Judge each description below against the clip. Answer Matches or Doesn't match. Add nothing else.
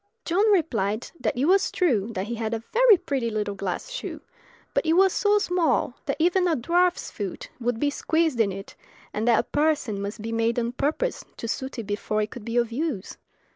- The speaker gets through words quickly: Matches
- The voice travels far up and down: Matches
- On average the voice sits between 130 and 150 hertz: Doesn't match